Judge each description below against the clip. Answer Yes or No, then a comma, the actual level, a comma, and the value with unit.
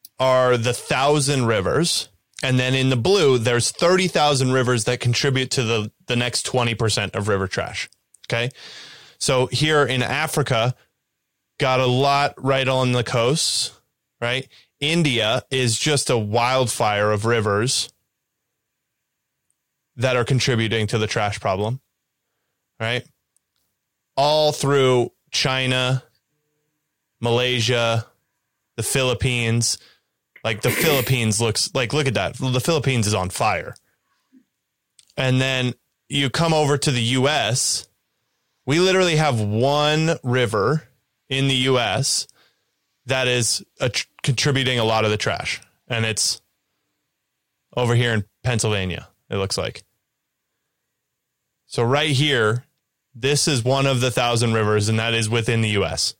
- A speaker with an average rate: No, slow, 130 wpm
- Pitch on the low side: Yes, low, 125 Hz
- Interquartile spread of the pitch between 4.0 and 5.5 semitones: No, average, 3.2 semitones